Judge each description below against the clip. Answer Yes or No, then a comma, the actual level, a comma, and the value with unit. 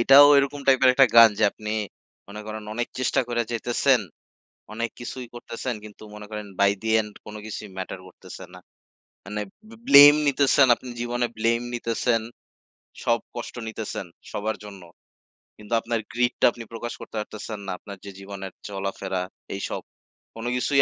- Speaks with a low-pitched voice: Yes, low, 115 Hz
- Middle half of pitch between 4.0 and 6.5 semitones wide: No, narrow, 2.5 semitones